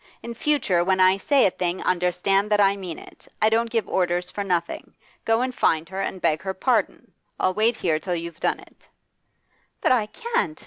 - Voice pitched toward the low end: No, high, 190 Hz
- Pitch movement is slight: No, average, 3.9 semitones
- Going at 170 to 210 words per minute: Yes, average, 200 wpm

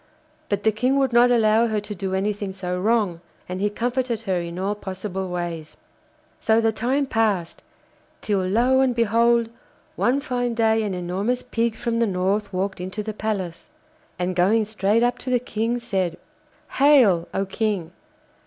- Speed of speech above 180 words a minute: No, average, 170 wpm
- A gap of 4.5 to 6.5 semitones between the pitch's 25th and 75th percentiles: No, average, 3.7 semitones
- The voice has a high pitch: Yes, high, 215 Hz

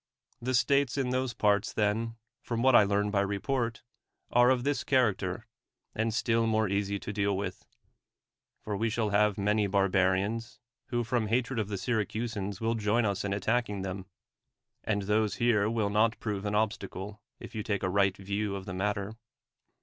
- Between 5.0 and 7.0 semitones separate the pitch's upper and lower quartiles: No, narrow, 2.4 semitones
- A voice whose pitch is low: Yes, low, 105 Hz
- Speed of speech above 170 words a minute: Yes, average, 185 wpm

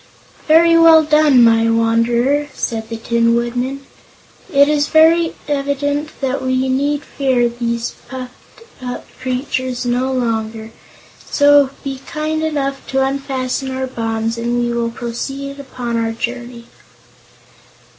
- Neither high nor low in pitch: No, very high, 260 Hz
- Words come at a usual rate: No, slow, 125 wpm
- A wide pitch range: No, average, 3.2 semitones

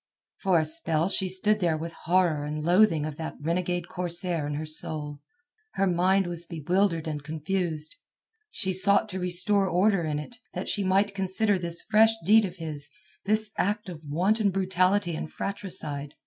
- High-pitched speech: No, medium, 180 Hz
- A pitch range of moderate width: Yes, average, 3.8 semitones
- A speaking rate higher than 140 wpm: Yes, average, 170 wpm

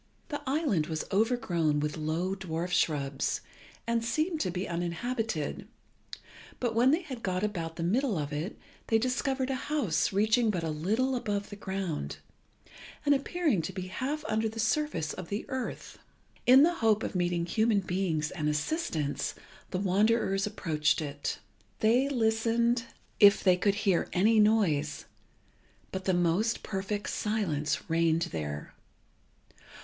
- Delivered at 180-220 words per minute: No, average, 145 wpm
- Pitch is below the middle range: No, high, 200 Hz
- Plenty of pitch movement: Yes, wide, 5.8 semitones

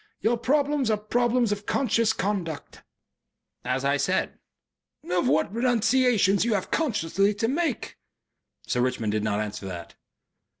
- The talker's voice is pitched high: Yes, high, 210 Hz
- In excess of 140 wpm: No, slow, 135 wpm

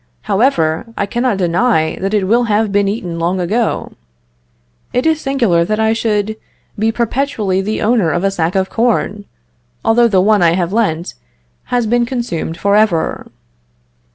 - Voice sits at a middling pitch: No, high, 210 Hz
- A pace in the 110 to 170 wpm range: Yes, average, 160 wpm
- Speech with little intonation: No, average, 4.2 semitones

